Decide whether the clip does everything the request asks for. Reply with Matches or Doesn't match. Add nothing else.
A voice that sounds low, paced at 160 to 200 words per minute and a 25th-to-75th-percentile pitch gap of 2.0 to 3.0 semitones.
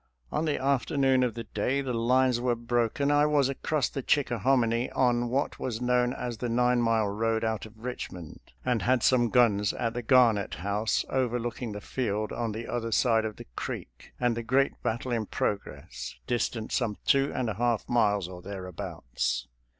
Matches